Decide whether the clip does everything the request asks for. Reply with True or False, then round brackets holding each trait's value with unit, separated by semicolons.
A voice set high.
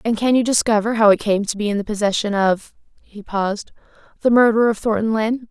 True (215 Hz)